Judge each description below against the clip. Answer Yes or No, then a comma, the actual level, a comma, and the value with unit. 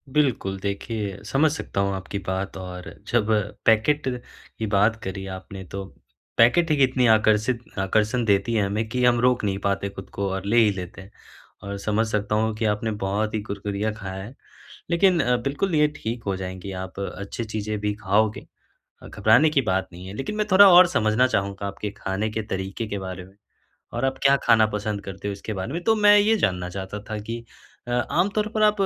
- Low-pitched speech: Yes, low, 105 Hz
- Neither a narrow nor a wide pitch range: Yes, average, 3.7 semitones